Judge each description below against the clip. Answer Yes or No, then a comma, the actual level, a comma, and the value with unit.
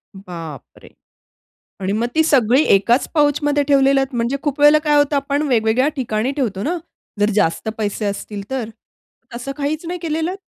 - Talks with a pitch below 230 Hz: No, very high, 265 Hz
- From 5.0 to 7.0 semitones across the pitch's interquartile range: Yes, average, 5.3 semitones